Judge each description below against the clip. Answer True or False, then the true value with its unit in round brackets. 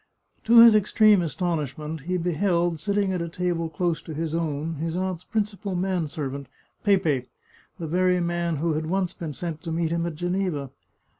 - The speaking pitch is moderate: True (170 Hz)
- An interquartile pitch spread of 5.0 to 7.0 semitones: False (2.5 semitones)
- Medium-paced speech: True (175 wpm)